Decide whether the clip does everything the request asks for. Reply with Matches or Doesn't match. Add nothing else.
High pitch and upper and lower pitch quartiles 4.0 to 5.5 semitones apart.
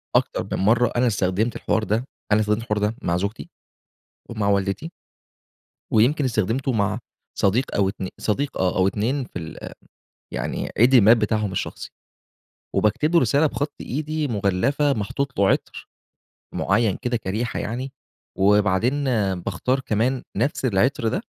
Doesn't match